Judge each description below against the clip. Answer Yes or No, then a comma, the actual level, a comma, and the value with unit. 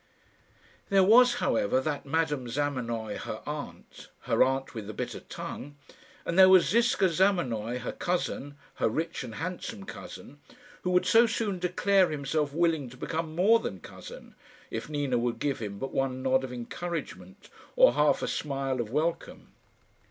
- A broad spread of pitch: Yes, wide, 6.1 semitones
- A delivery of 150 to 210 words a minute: Yes, average, 160 wpm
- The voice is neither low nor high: Yes, medium, 145 Hz